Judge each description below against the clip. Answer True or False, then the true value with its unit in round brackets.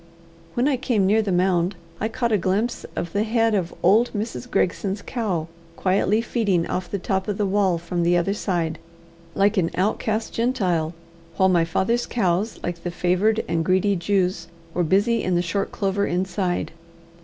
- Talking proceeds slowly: False (180 wpm)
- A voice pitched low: False (190 Hz)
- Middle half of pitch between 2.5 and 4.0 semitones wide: True (3.4 semitones)